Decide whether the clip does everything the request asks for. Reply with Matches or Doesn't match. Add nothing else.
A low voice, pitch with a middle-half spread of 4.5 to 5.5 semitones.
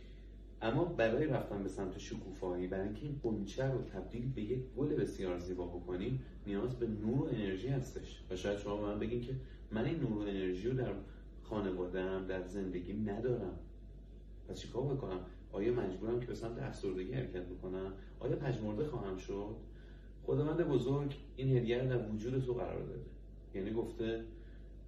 Matches